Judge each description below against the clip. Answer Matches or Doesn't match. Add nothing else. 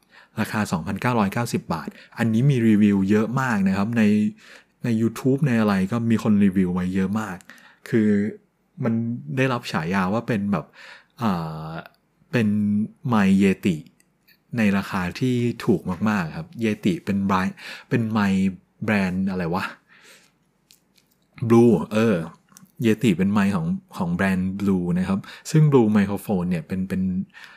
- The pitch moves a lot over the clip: Matches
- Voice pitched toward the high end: Doesn't match